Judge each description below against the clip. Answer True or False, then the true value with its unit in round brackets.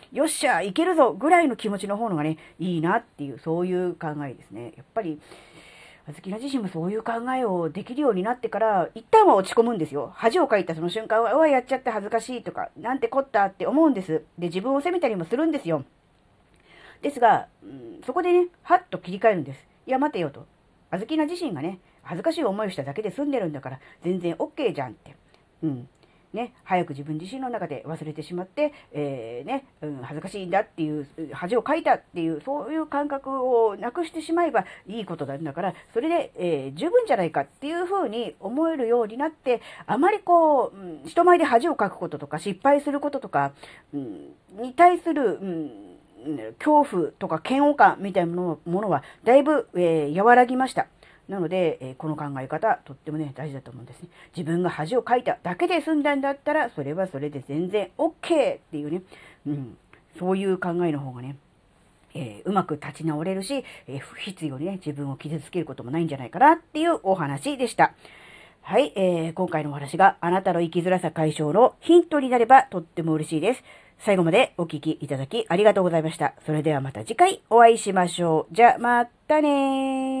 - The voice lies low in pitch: False (190 Hz)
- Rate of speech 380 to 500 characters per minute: True (410 characters per minute)